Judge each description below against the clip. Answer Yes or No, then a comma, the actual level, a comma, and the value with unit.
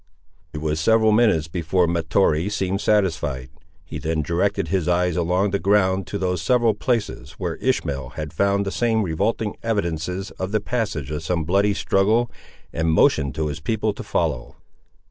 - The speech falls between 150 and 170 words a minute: Yes, average, 165 wpm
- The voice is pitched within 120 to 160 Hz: No, very low, 90 Hz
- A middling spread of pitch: Yes, average, 4.5 semitones